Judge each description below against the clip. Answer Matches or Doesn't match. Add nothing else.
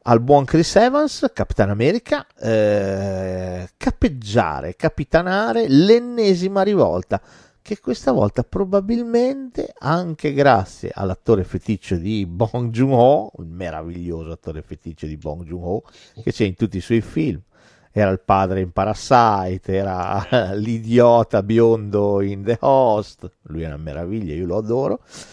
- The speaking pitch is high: Doesn't match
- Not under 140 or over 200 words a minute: Doesn't match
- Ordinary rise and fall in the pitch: Doesn't match